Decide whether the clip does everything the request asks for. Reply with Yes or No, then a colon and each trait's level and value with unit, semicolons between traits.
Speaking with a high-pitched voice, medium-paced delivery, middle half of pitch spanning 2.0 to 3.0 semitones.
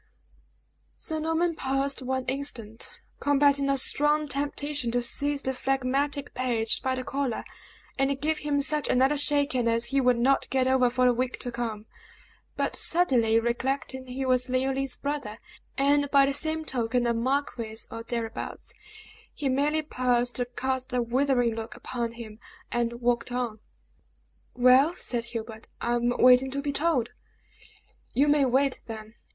Yes: very high, 260 Hz; average, 155 wpm; average, 2.7 semitones